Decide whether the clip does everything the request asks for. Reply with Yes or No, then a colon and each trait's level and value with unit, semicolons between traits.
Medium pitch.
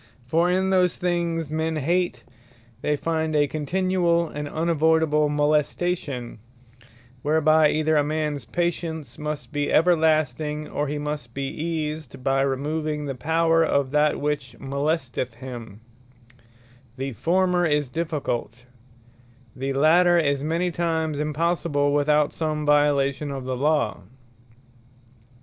Yes: medium, 150 Hz